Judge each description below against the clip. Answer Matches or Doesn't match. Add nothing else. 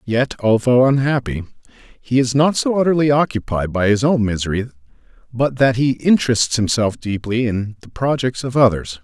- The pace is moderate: Matches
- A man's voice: Matches